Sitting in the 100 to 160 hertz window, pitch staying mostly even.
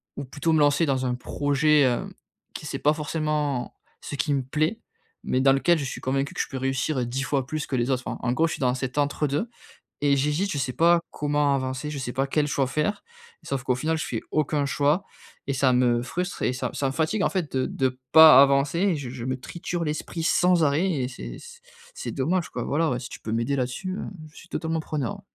No: medium, 140 Hz; average, 3.2 semitones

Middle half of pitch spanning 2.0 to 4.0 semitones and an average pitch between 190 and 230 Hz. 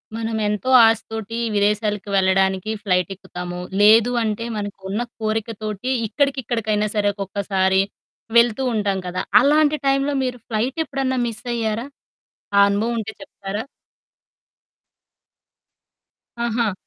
Yes: average, 2.8 semitones; high, 215 Hz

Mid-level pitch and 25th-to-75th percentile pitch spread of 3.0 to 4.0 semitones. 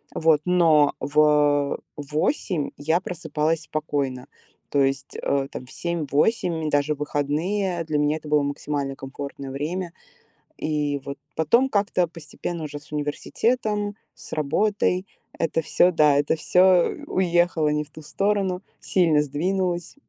Yes: medium, 155 Hz; average, 3.6 semitones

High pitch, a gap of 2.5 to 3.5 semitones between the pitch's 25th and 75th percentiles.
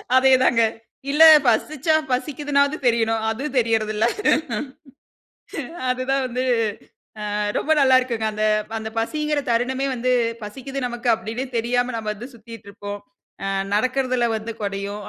Yes: high, 245 Hz; average, 3.1 semitones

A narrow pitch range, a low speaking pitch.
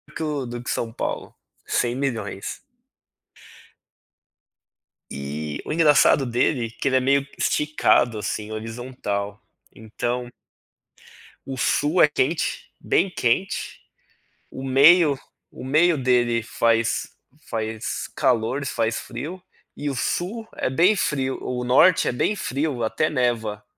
No: average, 4.4 semitones; low, 125 Hz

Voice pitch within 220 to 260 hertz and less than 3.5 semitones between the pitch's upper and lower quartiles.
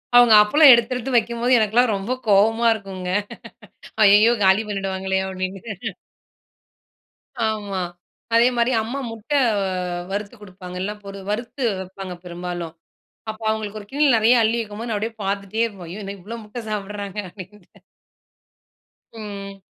No: high, 210 Hz; average, 3.0 semitones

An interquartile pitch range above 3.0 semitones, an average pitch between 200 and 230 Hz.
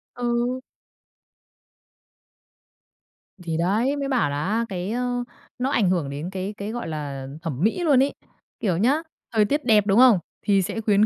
Yes: wide, 5.4 semitones; high, 215 Hz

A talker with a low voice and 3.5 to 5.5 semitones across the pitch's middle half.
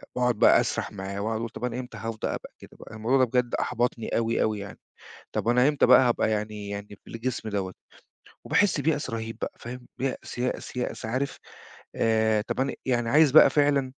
No: low, 120 Hz; average, 2.8 semitones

